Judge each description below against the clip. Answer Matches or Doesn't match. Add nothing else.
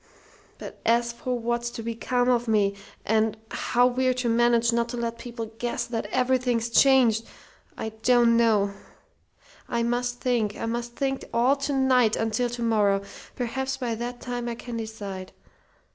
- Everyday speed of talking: Matches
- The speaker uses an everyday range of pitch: Doesn't match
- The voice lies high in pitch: Matches